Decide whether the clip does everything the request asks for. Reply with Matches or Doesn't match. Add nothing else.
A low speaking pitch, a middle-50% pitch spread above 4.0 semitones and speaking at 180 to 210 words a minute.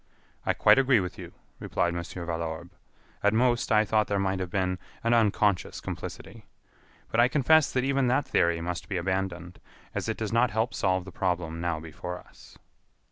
Matches